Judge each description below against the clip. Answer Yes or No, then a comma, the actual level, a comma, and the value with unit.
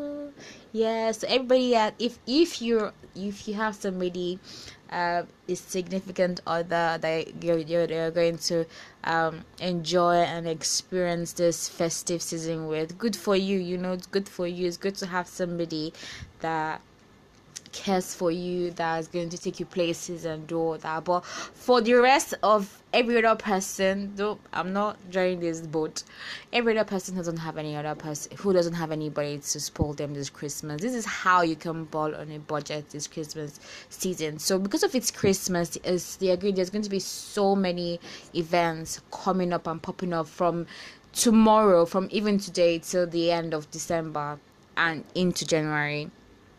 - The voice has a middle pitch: Yes, medium, 175 Hz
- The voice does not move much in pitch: No, average, 3.2 semitones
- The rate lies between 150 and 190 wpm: Yes, average, 170 wpm